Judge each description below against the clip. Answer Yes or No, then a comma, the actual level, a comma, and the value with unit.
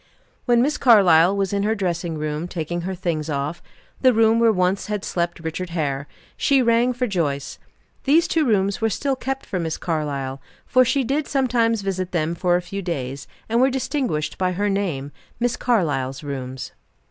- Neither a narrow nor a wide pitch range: No, wide, 6.5 semitones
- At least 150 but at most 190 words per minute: Yes, average, 180 wpm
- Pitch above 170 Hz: Yes, medium, 185 Hz